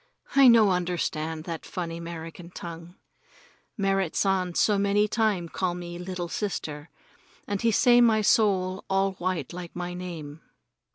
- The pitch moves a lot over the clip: No, average, 2.9 semitones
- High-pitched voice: No, medium, 180 Hz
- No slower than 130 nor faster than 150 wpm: Yes, average, 145 wpm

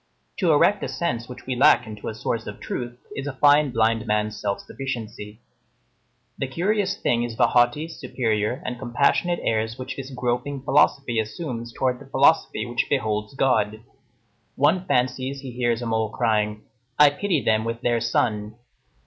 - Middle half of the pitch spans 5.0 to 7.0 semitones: No, average, 3.7 semitones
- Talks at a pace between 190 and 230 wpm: No, average, 165 wpm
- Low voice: Yes, low, 120 Hz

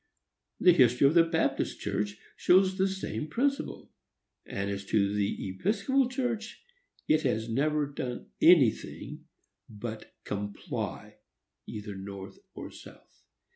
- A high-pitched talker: No, low, 135 Hz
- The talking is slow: Yes, slow, 120 wpm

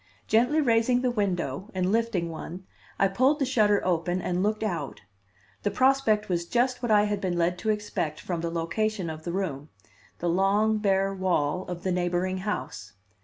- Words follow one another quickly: No, average, 180 wpm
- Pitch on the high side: Yes, high, 195 Hz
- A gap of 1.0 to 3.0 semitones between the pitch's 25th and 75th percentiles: No, average, 3.8 semitones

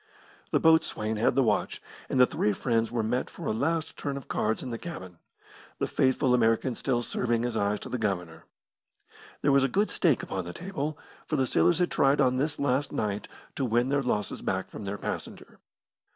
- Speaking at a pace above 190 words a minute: Yes, fast, 205 wpm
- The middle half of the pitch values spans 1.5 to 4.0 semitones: No, average, 4.4 semitones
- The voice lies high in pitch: No, low, 125 Hz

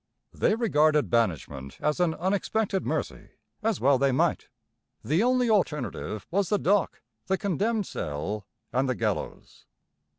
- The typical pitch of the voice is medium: Yes, medium, 155 Hz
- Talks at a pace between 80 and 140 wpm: Yes, slow, 135 wpm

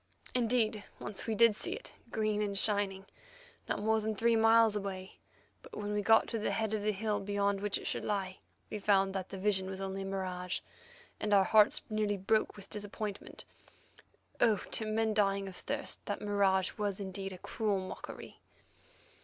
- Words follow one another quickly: No, average, 185 wpm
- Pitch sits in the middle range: No, high, 205 Hz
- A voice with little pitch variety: Yes, narrow, 1.9 semitones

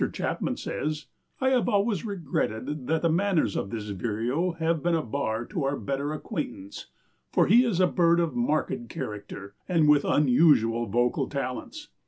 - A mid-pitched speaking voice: Yes, medium, 150 Hz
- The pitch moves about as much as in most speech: No, wide, 6.5 semitones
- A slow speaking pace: No, average, 165 wpm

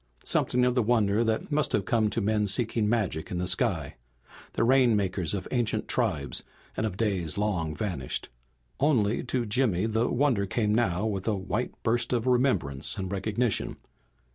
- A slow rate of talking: No, average, 165 wpm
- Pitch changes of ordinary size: Yes, average, 3.8 semitones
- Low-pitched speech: Yes, low, 105 Hz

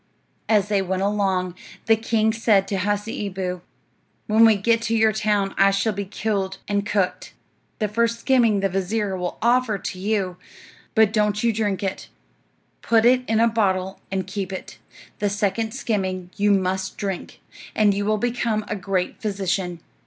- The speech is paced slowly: No, average, 165 wpm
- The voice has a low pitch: No, high, 205 Hz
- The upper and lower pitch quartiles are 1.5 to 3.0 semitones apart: Yes, narrow, 2.4 semitones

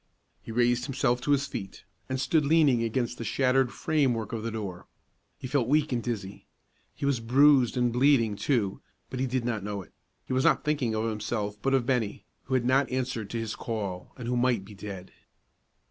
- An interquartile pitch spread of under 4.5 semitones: Yes, average, 3.2 semitones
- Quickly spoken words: Yes, fast, 210 wpm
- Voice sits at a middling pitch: No, low, 120 Hz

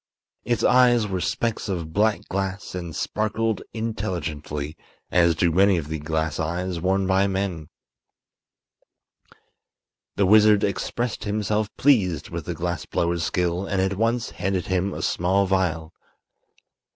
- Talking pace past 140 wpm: No, slow, 135 wpm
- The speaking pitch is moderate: No, very low, 95 Hz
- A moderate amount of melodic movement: Yes, average, 3.6 semitones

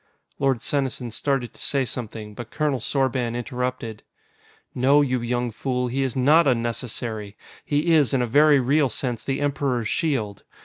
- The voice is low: Yes, low, 125 Hz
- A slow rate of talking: No, average, 160 wpm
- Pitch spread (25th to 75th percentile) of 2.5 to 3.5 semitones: Yes, average, 2.8 semitones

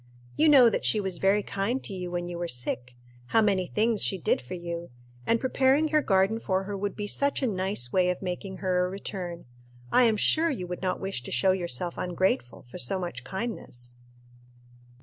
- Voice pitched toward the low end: No, high, 190 Hz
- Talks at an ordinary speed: No, fast, 210 wpm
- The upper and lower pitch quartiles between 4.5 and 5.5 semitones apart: No, average, 3.5 semitones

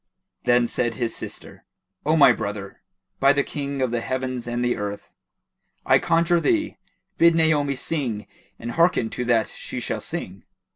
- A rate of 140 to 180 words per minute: Yes, average, 160 wpm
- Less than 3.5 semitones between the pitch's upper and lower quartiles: No, average, 4.5 semitones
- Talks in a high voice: No, low, 130 Hz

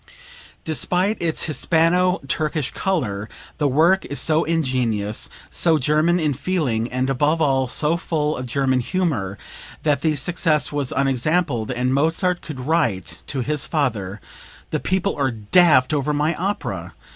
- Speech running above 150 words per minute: No, average, 145 wpm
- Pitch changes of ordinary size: Yes, average, 4.4 semitones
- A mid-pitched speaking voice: Yes, medium, 150 Hz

